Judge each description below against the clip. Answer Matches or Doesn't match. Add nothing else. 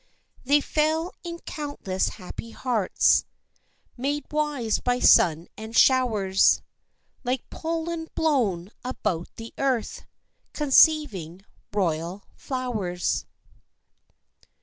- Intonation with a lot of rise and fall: Matches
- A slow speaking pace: Matches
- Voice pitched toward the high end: Matches